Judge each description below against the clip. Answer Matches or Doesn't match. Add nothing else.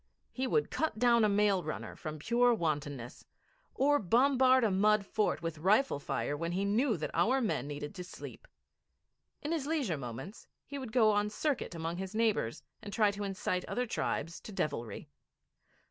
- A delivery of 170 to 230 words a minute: Matches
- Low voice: Doesn't match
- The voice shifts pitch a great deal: Matches